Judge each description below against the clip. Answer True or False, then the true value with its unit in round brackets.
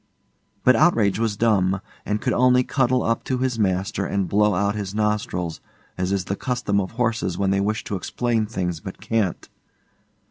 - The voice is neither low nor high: False (105 Hz)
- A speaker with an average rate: True (180 wpm)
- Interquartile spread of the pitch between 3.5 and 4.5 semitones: False (3.1 semitones)